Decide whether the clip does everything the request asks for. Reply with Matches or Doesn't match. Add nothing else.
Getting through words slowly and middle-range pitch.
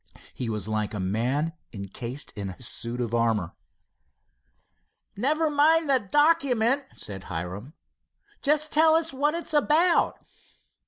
Matches